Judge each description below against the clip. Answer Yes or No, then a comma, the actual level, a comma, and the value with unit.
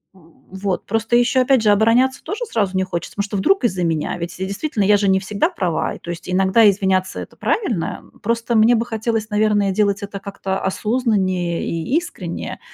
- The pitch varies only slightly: No, average, 3.3 semitones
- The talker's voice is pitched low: No, high, 200 Hz